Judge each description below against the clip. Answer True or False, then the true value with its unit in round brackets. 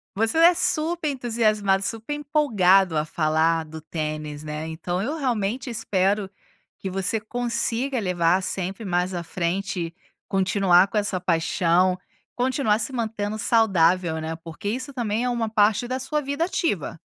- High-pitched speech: True (200 Hz)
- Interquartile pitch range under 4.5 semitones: False (5.5 semitones)